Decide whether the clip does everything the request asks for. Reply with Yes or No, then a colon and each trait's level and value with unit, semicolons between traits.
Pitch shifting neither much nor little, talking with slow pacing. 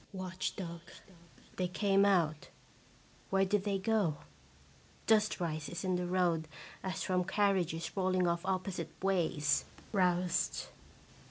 No: narrow, 2.1 semitones; slow, 120 wpm